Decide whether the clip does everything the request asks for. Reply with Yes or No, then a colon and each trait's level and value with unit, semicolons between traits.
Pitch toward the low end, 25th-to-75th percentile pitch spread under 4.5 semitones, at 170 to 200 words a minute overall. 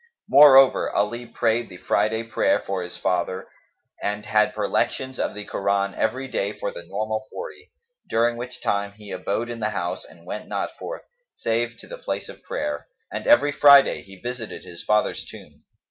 Yes: low, 110 Hz; average, 3.3 semitones; average, 175 wpm